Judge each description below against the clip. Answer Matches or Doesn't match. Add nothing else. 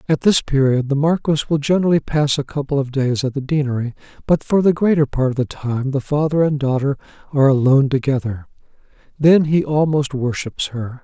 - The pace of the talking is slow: Doesn't match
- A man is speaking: Matches